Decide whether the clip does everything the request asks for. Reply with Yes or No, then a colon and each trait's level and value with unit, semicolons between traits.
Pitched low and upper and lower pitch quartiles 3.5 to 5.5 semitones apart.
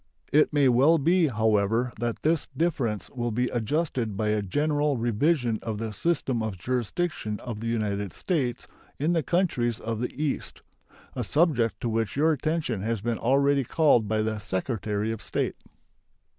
Yes: low, 120 Hz; average, 5.2 semitones